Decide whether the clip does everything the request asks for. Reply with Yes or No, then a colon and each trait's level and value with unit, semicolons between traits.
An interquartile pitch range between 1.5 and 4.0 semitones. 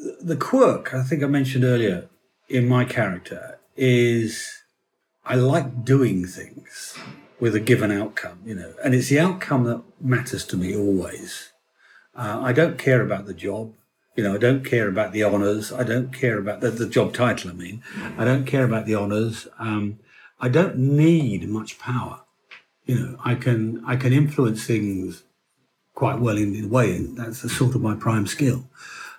Yes: average, 3.2 semitones